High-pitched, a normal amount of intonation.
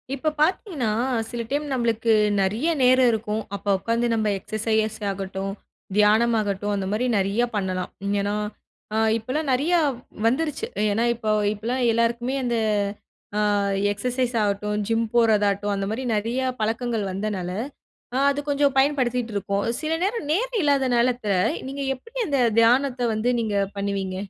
Yes: high, 230 Hz; average, 3.9 semitones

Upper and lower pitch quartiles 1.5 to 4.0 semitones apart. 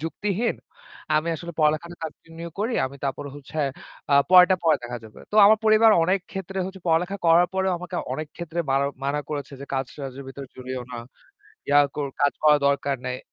No: average, 4.4 semitones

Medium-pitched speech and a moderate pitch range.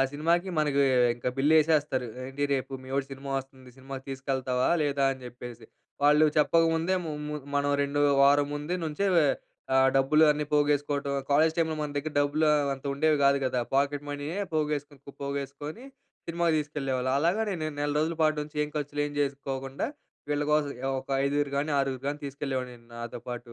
No: medium, 145 Hz; narrow, 2.0 semitones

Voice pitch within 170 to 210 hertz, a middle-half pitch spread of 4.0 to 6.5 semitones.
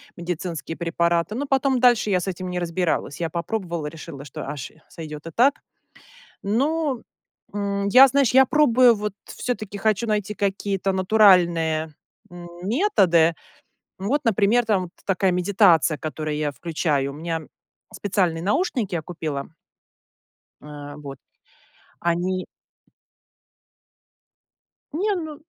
Yes: medium, 185 Hz; average, 5.1 semitones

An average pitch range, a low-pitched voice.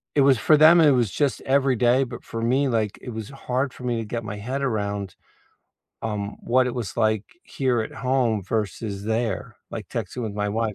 Yes: average, 3.4 semitones; low, 115 Hz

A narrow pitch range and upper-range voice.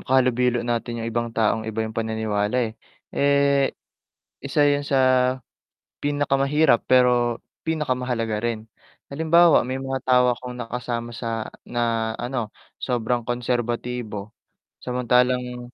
No: narrow, 2.3 semitones; low, 125 Hz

